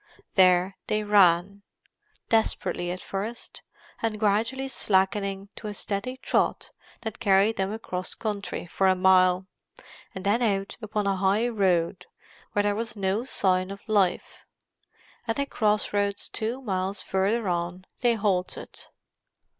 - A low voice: No, high, 200 Hz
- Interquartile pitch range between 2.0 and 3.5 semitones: Yes, narrow, 2.5 semitones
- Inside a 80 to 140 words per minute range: Yes, slow, 135 wpm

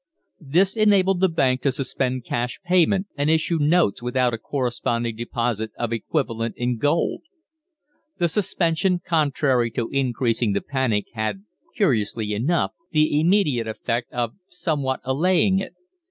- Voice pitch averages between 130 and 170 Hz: Yes, low, 135 Hz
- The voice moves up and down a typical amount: No, wide, 6.2 semitones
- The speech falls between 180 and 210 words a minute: No, average, 140 wpm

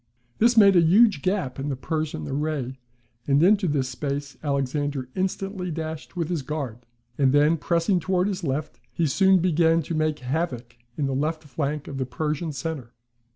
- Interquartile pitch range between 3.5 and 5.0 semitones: Yes, average, 3.9 semitones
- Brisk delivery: No, average, 175 wpm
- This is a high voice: No, medium, 155 Hz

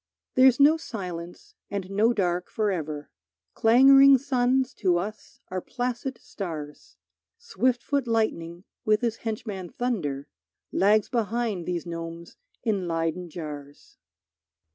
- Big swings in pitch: Yes, wide, 6.0 semitones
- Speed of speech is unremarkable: No, slow, 115 wpm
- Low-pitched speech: No, high, 205 Hz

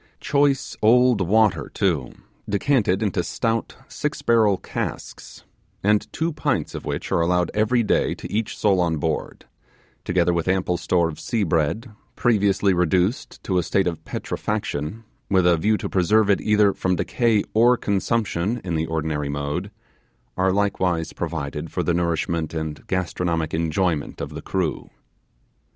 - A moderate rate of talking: Yes, average, 150 wpm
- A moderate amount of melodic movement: Yes, average, 4.3 semitones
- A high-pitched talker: No, very low, 95 Hz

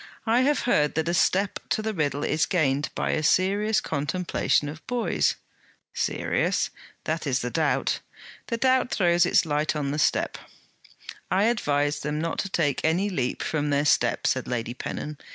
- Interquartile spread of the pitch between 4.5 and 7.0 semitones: Yes, average, 5.3 semitones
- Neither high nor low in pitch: Yes, medium, 160 Hz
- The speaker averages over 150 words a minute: Yes, average, 170 wpm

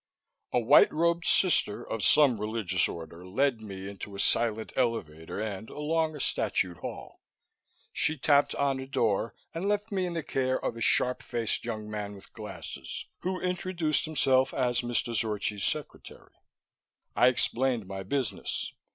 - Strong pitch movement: Yes, wide, 6.1 semitones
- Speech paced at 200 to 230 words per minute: No, average, 155 wpm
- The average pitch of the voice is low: Yes, low, 120 Hz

